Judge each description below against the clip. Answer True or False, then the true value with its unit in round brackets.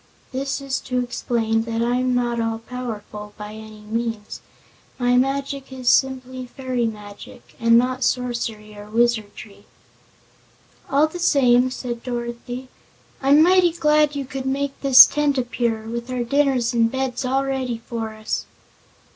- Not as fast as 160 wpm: True (145 wpm)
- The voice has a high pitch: True (245 Hz)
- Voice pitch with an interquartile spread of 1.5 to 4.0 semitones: True (2.7 semitones)